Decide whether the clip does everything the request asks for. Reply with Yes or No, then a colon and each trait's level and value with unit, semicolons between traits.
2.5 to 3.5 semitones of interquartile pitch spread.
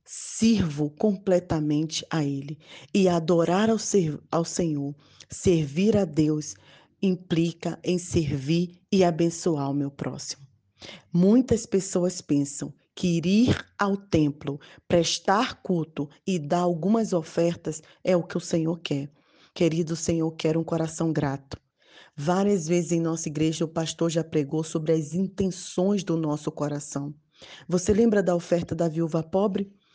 Yes: average, 2.8 semitones